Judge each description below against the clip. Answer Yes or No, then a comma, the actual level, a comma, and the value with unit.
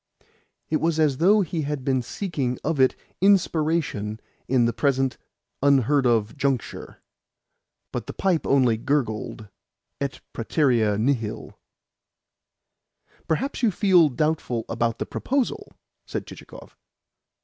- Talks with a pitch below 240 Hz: Yes, medium, 140 Hz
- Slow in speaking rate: Yes, slow, 115 wpm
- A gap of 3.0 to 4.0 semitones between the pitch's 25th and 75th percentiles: No, average, 5.2 semitones